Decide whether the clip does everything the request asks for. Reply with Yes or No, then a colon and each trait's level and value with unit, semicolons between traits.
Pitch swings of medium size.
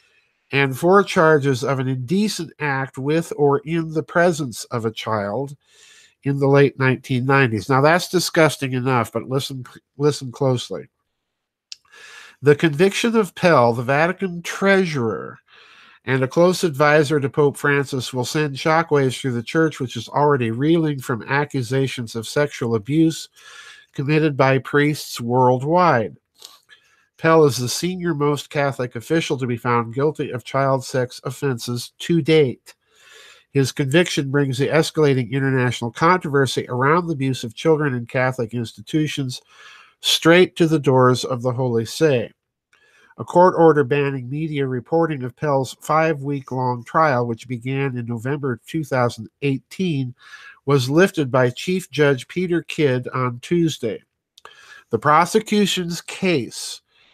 Yes: average, 4.0 semitones